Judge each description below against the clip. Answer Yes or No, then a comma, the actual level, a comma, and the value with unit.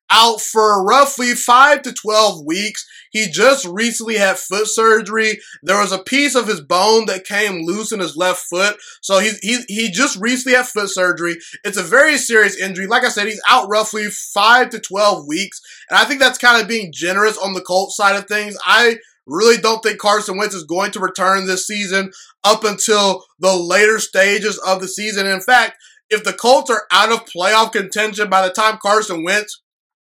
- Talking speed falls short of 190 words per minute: No, average, 200 wpm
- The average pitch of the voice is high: Yes, high, 210 Hz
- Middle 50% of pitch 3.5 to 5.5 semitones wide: No, average, 2.7 semitones